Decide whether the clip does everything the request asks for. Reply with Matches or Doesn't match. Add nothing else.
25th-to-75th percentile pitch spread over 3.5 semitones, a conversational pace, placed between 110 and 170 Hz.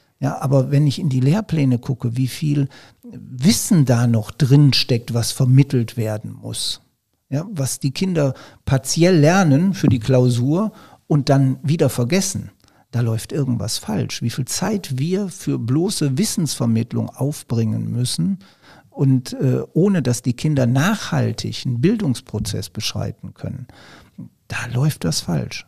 Matches